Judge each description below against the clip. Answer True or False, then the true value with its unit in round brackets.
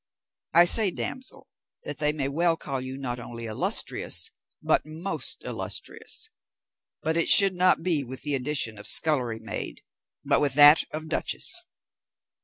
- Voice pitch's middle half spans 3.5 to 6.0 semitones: True (4.4 semitones)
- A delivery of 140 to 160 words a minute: True (150 wpm)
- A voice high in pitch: False (150 Hz)